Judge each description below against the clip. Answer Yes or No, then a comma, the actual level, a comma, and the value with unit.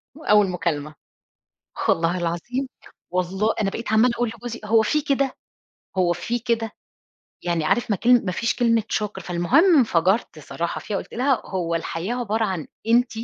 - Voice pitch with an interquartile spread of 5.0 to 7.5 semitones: Yes, wide, 5.4 semitones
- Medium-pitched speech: No, high, 215 Hz